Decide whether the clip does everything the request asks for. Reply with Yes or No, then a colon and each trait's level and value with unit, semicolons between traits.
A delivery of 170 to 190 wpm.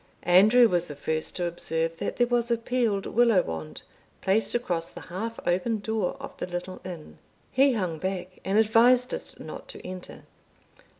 Yes: average, 175 wpm